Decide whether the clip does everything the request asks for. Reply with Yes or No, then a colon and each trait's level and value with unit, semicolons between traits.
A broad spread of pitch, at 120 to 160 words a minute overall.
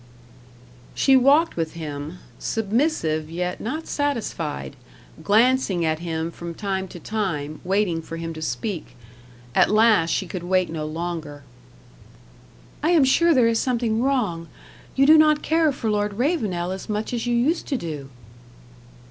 Yes: wide, 7.3 semitones; average, 150 wpm